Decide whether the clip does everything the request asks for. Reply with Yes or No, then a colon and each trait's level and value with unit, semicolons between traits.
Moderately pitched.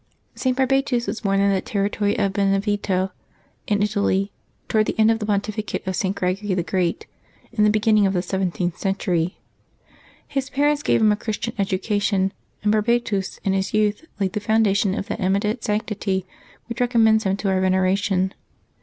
No: high, 205 Hz